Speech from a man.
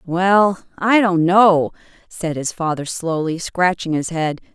No: female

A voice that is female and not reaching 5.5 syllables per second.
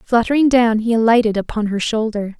No: female; 5.6 syllables/s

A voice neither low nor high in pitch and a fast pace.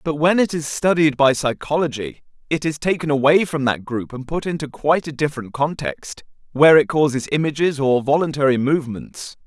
No: medium, 145 Hz; average, 180 wpm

